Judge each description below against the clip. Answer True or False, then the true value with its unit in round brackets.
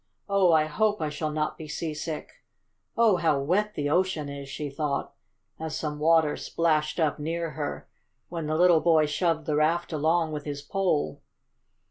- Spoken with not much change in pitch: True (2.1 semitones)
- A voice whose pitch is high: False (155 Hz)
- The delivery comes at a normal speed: True (170 wpm)